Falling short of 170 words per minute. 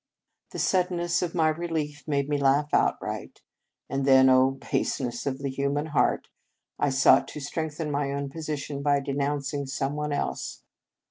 Yes: average, 155 wpm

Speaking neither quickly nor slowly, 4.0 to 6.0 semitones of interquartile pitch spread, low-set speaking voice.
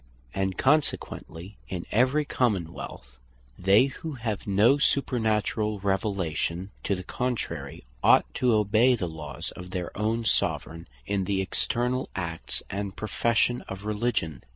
No: slow, 130 wpm; average, 4.4 semitones; low, 105 Hz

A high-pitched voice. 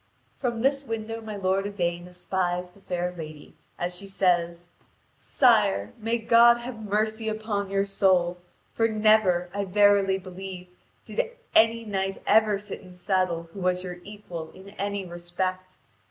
Yes: high, 195 Hz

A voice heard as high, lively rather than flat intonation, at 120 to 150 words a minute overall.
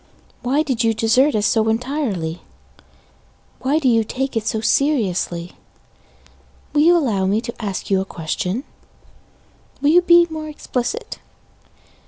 Yes: high, 235 Hz; wide, 5.8 semitones; average, 140 wpm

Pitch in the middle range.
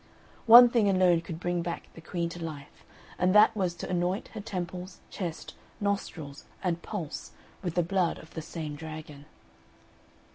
Yes: medium, 175 Hz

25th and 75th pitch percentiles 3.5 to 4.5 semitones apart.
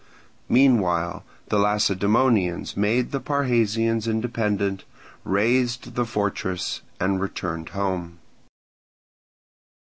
Yes: average, 3.8 semitones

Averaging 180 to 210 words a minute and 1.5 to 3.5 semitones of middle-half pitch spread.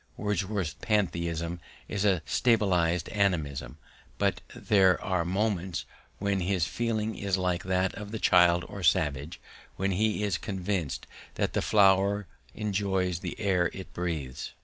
No: slow, 135 wpm; average, 2.8 semitones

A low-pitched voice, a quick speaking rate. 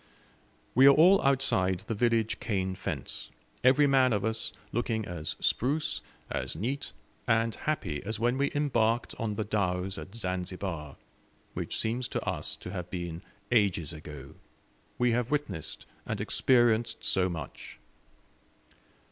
No: low, 110 Hz; average, 140 wpm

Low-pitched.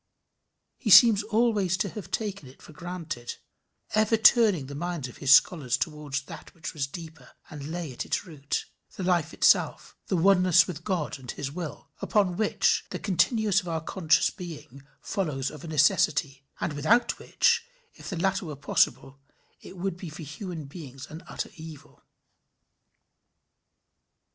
No: medium, 165 Hz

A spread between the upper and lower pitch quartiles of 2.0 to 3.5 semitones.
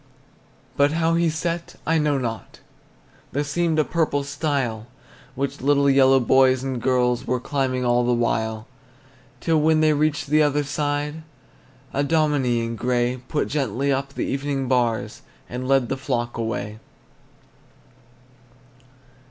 Yes: average, 3.2 semitones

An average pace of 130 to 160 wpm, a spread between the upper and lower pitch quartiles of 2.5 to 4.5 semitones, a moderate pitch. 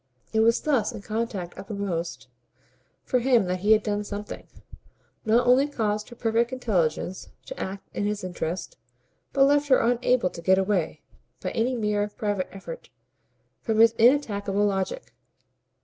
No: average, 150 wpm; average, 3.7 semitones; high, 210 Hz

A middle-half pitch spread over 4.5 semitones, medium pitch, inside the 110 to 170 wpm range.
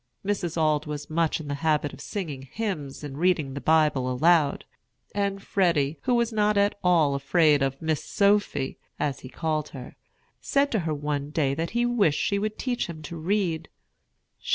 No: wide, 5.5 semitones; medium, 160 Hz; average, 180 wpm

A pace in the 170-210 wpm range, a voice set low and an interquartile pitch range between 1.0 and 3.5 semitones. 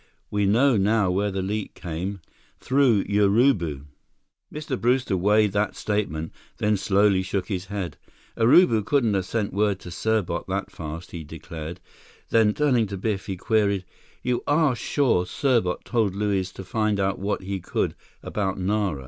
No: average, 155 wpm; low, 100 Hz; average, 2.9 semitones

